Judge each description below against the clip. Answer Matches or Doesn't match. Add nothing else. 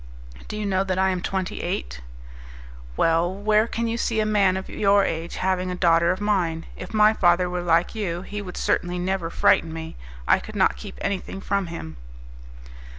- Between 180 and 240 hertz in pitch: Matches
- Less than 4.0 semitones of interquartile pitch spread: Matches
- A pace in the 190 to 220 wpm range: Matches